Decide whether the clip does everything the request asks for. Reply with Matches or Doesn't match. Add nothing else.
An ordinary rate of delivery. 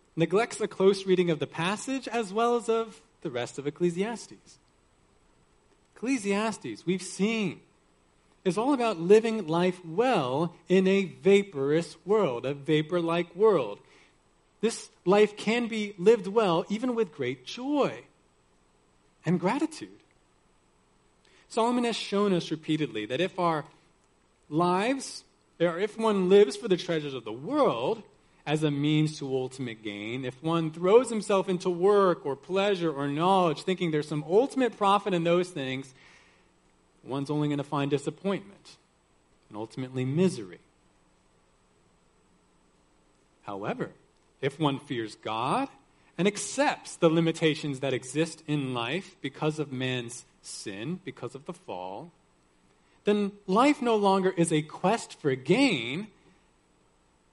Doesn't match